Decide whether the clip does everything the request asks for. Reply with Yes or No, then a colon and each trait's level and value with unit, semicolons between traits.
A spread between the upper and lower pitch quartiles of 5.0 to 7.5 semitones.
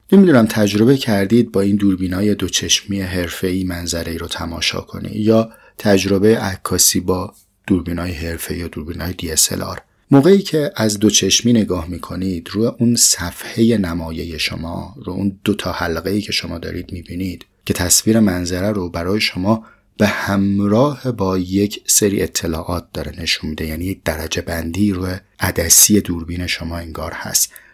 No: average, 3.4 semitones